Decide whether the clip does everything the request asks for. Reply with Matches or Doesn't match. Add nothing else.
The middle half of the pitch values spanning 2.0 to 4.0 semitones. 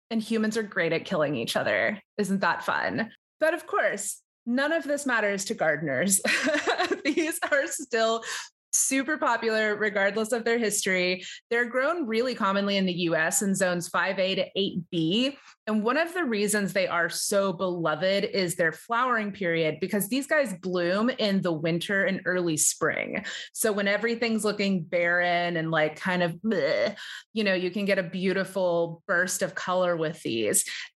Doesn't match